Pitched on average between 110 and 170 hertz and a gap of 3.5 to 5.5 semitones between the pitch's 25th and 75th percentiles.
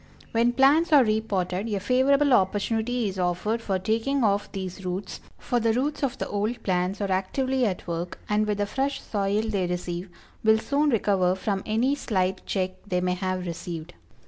No: high, 205 Hz; average, 4.4 semitones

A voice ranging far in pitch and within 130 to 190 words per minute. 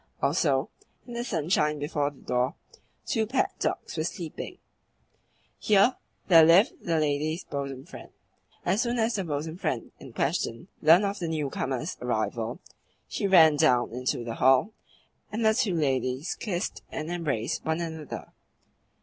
Yes: wide, 5.8 semitones; average, 150 wpm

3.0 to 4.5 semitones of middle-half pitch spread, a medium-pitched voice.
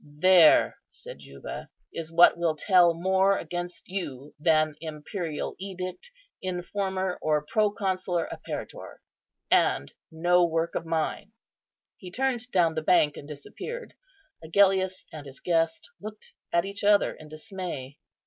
Yes: average, 3.3 semitones; medium, 175 Hz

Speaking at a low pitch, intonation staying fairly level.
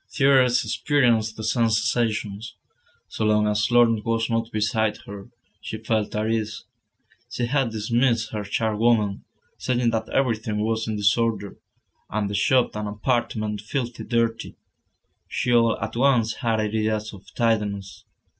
Yes: low, 110 Hz; narrow, 1.8 semitones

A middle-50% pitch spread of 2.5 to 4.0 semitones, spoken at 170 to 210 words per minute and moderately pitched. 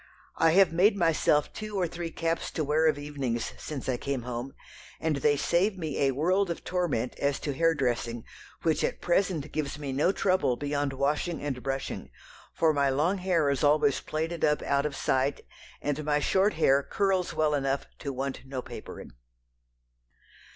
Yes: average, 3.4 semitones; average, 180 wpm; medium, 150 Hz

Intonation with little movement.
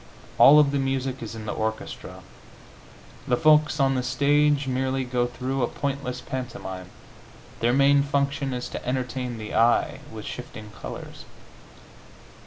Yes: narrow, 2.3 semitones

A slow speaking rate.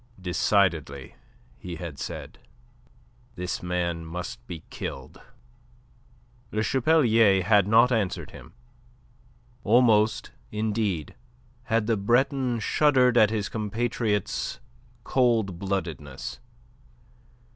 Yes: slow, 90 wpm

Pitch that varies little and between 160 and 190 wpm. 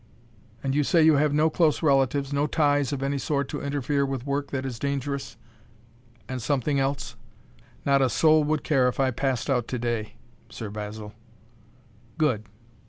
Yes: narrow, 2.3 semitones; average, 170 wpm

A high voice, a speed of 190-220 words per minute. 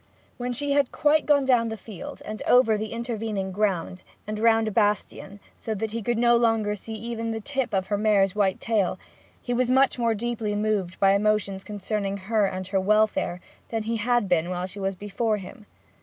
Yes: high, 215 Hz; average, 200 wpm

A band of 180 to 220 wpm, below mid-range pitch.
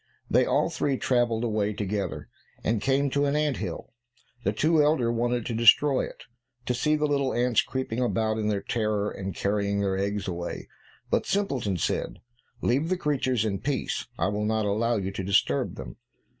Yes: average, 185 wpm; low, 110 Hz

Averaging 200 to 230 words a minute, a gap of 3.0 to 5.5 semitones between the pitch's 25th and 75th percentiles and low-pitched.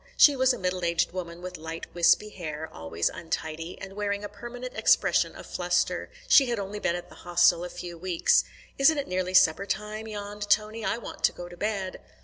No: fast, 205 wpm; average, 3.6 semitones; medium, 185 Hz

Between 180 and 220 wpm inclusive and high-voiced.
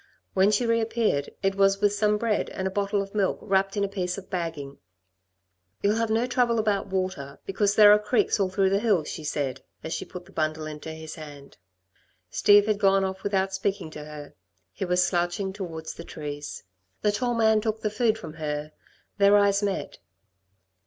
Yes: average, 195 wpm; high, 195 Hz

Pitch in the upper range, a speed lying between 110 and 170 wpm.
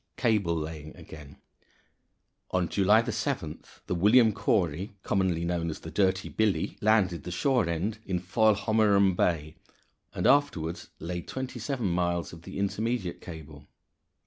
No: very low, 95 Hz; slow, 135 wpm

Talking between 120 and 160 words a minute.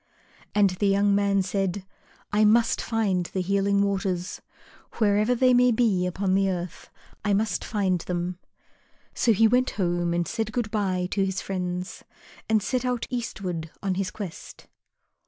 Yes: average, 155 wpm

